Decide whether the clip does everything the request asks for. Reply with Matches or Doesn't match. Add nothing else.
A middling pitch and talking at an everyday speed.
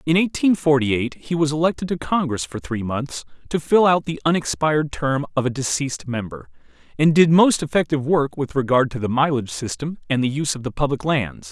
Doesn't match